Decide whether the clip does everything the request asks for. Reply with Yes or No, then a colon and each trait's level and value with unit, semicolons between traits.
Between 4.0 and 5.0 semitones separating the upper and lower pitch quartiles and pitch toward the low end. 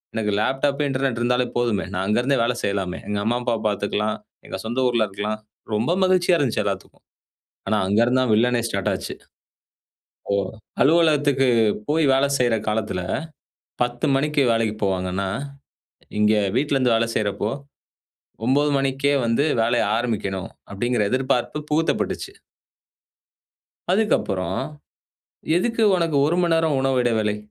Yes: average, 4.7 semitones; low, 120 Hz